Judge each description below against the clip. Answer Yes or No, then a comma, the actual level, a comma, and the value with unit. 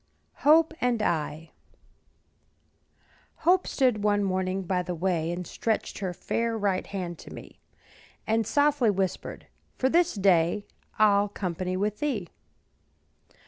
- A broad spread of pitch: No, average, 4.1 semitones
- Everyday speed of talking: No, slow, 125 wpm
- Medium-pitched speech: No, high, 200 Hz